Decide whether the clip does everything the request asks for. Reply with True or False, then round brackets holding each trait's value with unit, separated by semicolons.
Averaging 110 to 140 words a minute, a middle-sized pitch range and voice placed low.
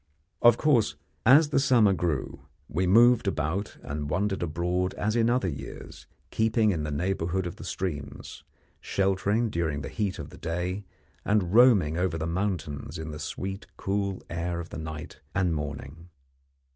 False (160 wpm; 4.6 semitones; 90 Hz)